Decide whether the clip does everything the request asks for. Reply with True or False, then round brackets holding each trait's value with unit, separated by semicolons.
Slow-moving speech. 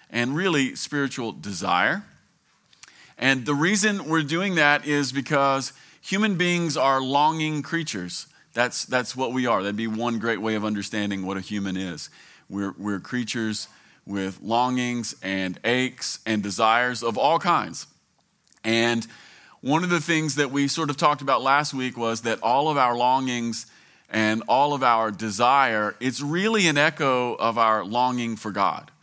False (160 wpm)